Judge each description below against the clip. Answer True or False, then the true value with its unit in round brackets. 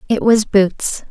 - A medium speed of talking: True (160 wpm)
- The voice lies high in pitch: True (210 Hz)